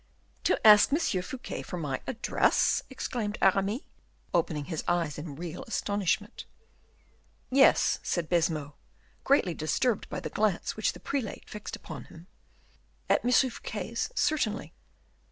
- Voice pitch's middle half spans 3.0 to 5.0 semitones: No, wide, 5.5 semitones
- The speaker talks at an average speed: No, slow, 130 wpm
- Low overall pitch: No, high, 195 Hz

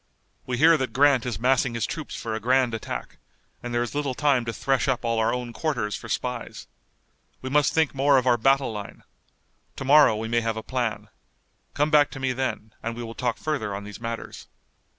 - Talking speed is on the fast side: Yes, fast, 215 wpm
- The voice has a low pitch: Yes, low, 125 Hz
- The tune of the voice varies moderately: Yes, average, 3.0 semitones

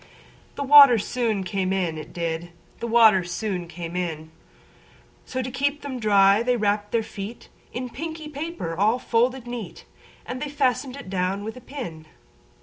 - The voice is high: Yes, high, 220 Hz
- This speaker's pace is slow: No, average, 160 wpm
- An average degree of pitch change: No, wide, 5.7 semitones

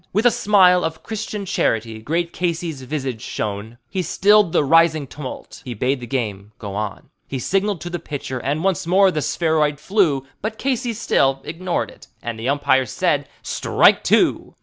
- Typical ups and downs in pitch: No, wide, 6.1 semitones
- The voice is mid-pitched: Yes, medium, 155 Hz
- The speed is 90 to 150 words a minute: No, average, 175 wpm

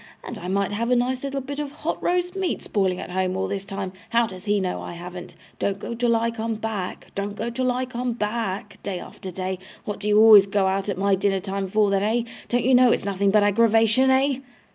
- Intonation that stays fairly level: No, average, 3.6 semitones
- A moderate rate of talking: No, fast, 245 wpm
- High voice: Yes, high, 210 Hz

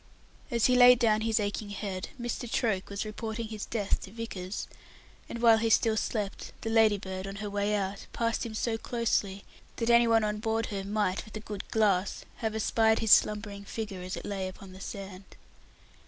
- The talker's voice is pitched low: No, high, 215 Hz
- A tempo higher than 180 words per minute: Yes, average, 195 wpm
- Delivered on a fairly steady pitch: Yes, narrow, 2.2 semitones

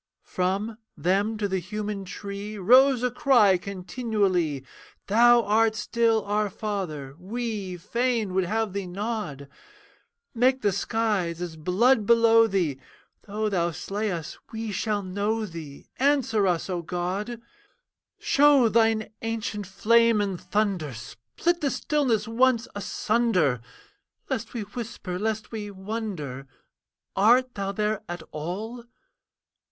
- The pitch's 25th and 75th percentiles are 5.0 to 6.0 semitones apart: No, average, 3.7 semitones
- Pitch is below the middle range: No, high, 210 Hz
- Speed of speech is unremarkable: No, slow, 125 wpm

